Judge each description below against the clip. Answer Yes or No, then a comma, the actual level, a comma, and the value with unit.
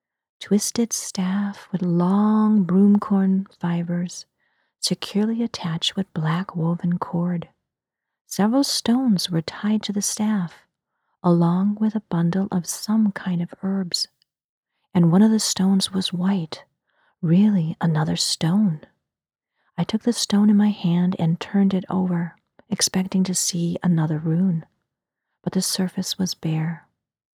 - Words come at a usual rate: No, slow, 130 wpm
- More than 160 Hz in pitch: Yes, medium, 185 Hz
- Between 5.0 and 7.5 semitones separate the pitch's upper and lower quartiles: No, average, 2.9 semitones